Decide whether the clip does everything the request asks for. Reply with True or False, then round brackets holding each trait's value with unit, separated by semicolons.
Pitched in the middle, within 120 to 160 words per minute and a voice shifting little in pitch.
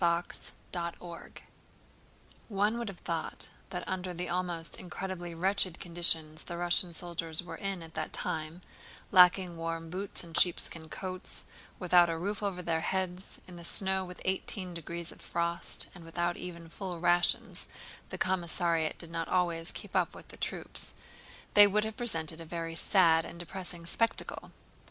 True (175 Hz; 155 wpm; 2.0 semitones)